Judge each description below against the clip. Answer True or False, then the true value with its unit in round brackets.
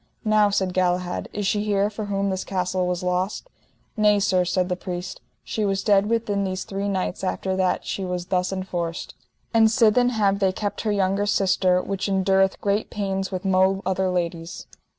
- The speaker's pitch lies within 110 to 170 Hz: False (190 Hz)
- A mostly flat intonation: True (1.7 semitones)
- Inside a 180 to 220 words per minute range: True (185 wpm)